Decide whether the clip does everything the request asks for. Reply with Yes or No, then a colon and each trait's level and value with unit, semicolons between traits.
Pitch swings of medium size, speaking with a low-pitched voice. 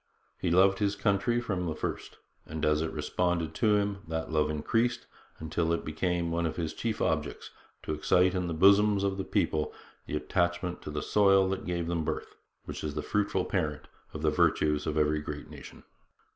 Yes: average, 3.9 semitones; very low, 85 Hz